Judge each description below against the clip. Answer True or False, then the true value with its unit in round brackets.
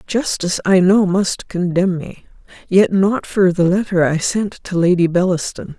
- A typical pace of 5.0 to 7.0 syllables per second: False (4.5 syllables/s)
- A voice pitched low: False (185 Hz)